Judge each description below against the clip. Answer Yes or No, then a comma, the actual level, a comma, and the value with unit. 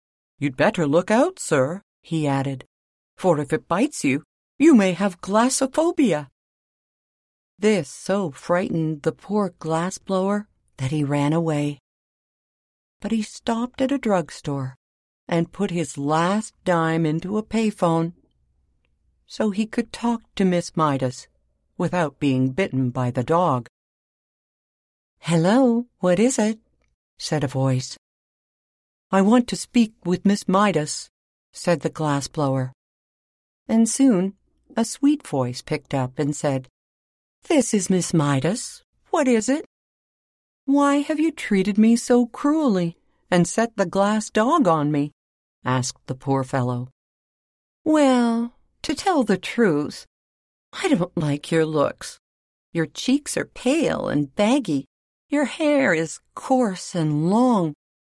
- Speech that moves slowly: Yes, slow, 130 wpm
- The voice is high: No, medium, 175 Hz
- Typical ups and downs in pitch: No, wide, 8.0 semitones